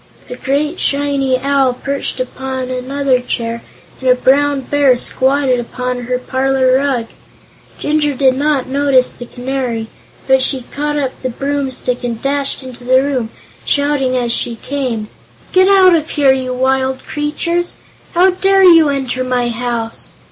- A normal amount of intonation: No, narrow, 2.2 semitones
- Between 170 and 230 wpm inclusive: No, average, 150 wpm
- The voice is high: Yes, very high, 265 Hz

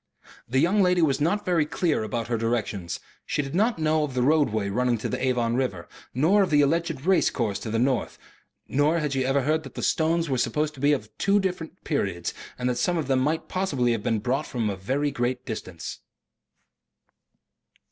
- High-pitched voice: No, low, 135 Hz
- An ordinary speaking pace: No, fast, 210 wpm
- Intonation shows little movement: No, average, 4.9 semitones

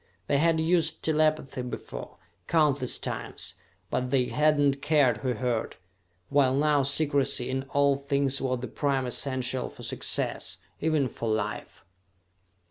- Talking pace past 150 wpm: No, slow, 135 wpm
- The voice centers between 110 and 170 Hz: Yes, medium, 140 Hz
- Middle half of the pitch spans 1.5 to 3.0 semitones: Yes, average, 2.7 semitones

